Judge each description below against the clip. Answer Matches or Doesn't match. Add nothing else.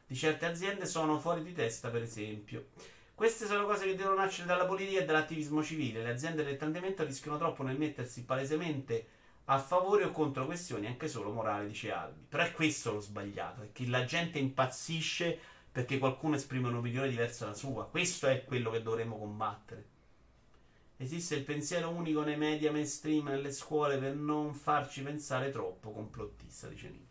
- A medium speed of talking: Doesn't match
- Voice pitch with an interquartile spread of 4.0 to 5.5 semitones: Matches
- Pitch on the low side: Doesn't match